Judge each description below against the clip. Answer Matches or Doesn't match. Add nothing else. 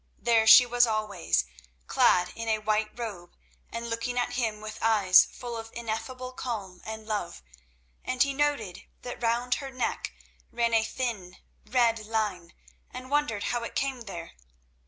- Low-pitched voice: Doesn't match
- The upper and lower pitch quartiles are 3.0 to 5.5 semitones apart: Doesn't match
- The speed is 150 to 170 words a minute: Matches